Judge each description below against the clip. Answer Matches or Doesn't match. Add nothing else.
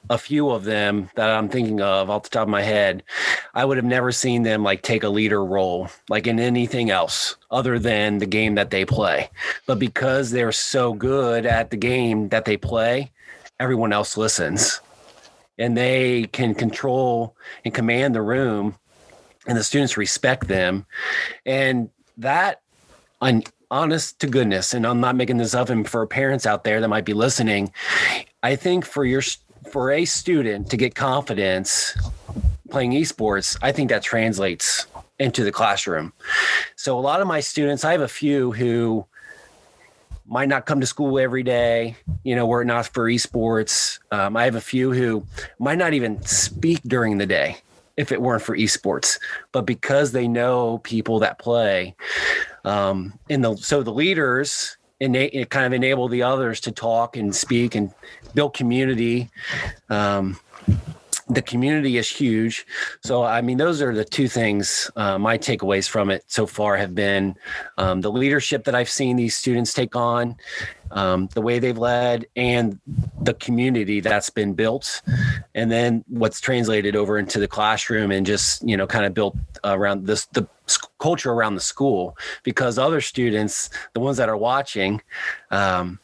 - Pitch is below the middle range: Matches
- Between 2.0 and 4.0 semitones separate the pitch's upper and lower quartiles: Matches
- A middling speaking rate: Matches